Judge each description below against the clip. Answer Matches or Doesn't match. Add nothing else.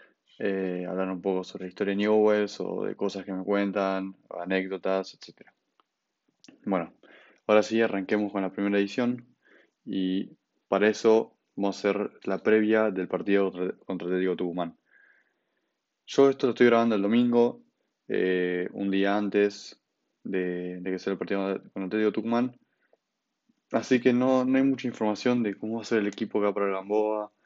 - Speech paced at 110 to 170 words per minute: Doesn't match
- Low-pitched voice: Matches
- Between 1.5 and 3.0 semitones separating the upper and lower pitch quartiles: Matches